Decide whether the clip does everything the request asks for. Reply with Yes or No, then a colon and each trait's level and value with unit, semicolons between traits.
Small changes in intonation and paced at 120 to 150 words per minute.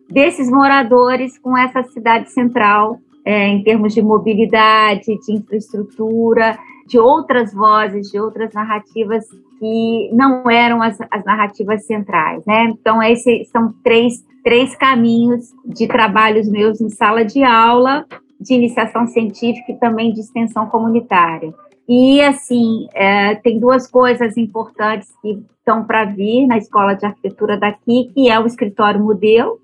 Yes: narrow, 2.1 semitones; average, 140 wpm